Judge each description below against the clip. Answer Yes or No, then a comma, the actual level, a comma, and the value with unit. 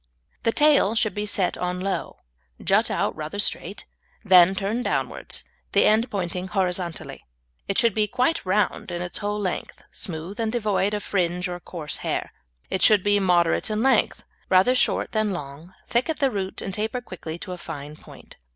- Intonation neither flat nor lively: Yes, average, 3.3 semitones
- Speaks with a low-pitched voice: No, high, 195 Hz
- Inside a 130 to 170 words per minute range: No, average, 180 wpm